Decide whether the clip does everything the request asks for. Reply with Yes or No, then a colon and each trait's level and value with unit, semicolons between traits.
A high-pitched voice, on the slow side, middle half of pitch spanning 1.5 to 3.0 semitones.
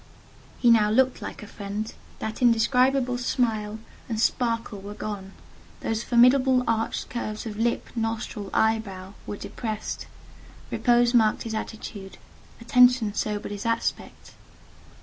Yes: high, 225 Hz; slow, 120 wpm; narrow, 2.4 semitones